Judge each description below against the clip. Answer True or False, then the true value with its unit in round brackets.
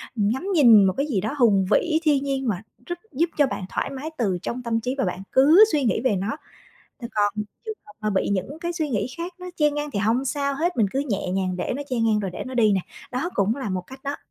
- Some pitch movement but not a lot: False (6.0 semitones)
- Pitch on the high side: True (250 Hz)